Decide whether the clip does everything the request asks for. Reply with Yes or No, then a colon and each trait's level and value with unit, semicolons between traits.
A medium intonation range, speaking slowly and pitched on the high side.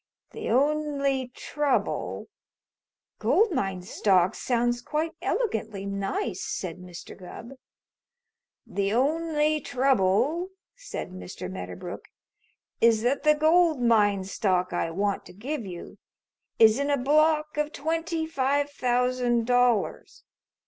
No: wide, 7.2 semitones; slow, 115 wpm; very high, 250 Hz